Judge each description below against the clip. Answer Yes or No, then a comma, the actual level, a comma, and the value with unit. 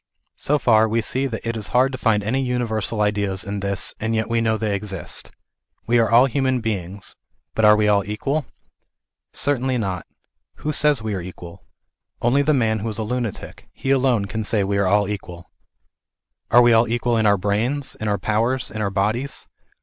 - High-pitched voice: No, low, 110 Hz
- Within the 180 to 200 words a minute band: Yes, average, 195 wpm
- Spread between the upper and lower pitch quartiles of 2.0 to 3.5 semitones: Yes, average, 3.2 semitones